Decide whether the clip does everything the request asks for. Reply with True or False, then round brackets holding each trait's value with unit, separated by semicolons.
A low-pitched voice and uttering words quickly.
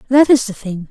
False (230 Hz; 265 wpm)